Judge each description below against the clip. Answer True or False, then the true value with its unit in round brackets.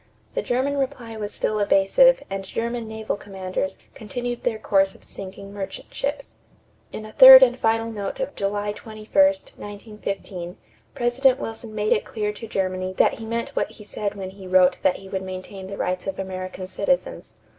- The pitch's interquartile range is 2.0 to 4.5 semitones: True (3.4 semitones)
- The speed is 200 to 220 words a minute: False (175 wpm)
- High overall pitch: True (210 Hz)